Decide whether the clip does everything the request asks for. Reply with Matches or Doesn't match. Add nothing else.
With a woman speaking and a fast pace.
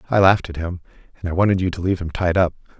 Doesn't match